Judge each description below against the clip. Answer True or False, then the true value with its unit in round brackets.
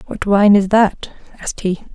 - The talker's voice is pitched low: False (200 Hz)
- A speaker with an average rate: True (185 wpm)